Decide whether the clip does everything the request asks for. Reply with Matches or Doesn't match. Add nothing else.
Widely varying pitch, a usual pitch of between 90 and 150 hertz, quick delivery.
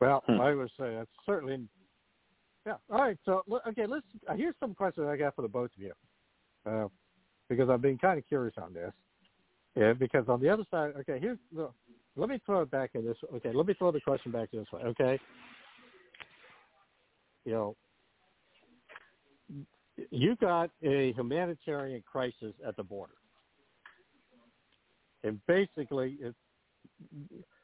Doesn't match